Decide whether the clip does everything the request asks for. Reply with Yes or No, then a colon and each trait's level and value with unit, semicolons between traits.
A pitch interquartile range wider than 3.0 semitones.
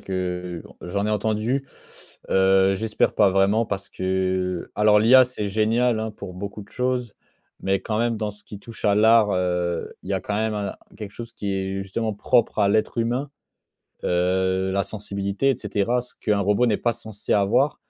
No: average, 2.7 semitones